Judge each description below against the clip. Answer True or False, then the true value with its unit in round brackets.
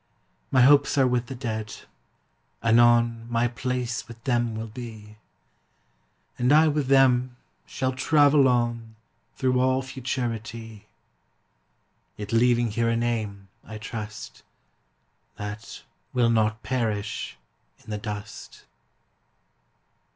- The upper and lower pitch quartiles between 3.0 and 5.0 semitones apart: False (2.5 semitones)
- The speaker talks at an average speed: False (110 wpm)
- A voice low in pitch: True (120 Hz)